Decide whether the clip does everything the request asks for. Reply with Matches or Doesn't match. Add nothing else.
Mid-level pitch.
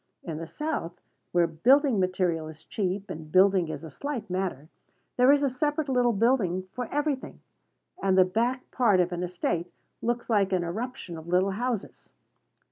Doesn't match